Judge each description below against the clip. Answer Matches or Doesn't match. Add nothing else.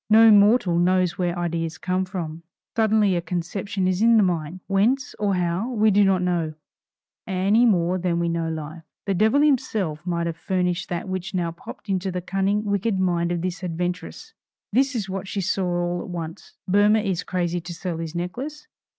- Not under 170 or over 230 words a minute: Matches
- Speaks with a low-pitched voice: Doesn't match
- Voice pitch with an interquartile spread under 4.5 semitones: Matches